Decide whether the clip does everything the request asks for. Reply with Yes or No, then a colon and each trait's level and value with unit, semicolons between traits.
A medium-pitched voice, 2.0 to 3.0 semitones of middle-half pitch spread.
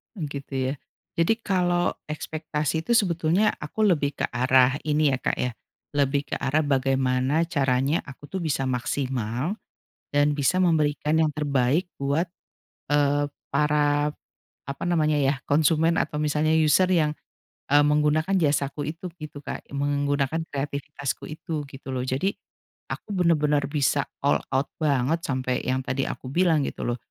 Yes: medium, 145 Hz; narrow, 2.5 semitones